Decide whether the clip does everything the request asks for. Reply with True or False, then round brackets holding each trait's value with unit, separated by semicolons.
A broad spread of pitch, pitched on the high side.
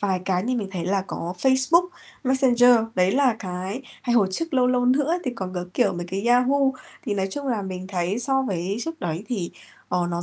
True (5.9 semitones; 210 Hz)